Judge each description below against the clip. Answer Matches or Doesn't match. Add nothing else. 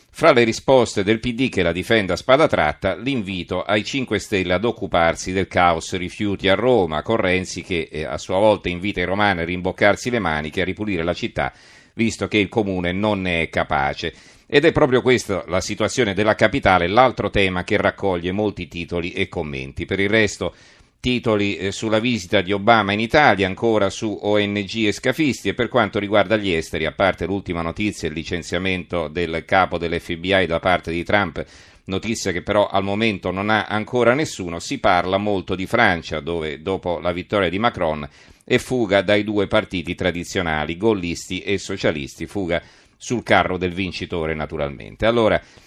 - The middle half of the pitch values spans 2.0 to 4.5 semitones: Matches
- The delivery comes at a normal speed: Doesn't match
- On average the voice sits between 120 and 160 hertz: Doesn't match